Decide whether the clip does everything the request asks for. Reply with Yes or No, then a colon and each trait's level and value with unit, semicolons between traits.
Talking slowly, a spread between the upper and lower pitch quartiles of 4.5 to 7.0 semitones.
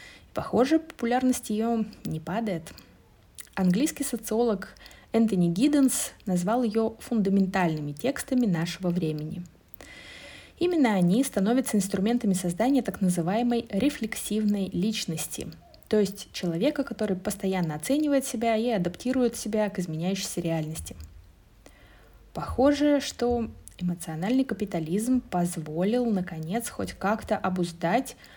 Yes: slow, 95 wpm; average, 5.3 semitones